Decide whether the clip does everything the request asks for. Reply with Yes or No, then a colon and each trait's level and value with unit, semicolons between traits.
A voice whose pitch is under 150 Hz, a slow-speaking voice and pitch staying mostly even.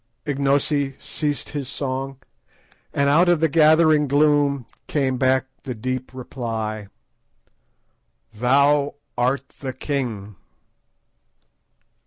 Yes: low, 135 Hz; slow, 95 wpm; narrow, 2.2 semitones